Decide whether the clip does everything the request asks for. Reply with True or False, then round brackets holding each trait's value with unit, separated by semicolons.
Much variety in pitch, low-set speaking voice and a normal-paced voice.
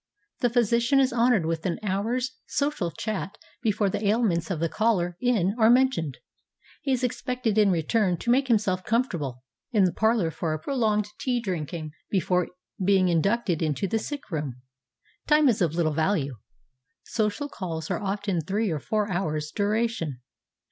False (5.8 semitones; 200 Hz; 170 wpm)